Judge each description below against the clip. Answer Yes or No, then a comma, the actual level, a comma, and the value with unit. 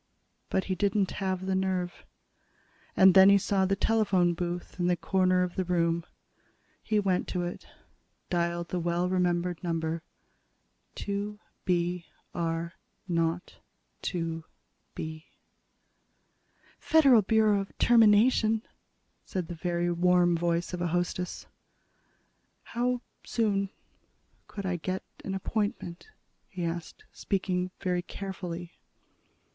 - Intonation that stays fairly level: Yes, narrow, 2.2 semitones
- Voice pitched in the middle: Yes, medium, 180 Hz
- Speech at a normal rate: No, slow, 120 wpm